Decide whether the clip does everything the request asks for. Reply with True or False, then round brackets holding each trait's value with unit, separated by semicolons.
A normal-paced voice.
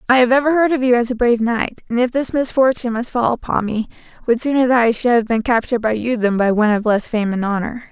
False (275 wpm)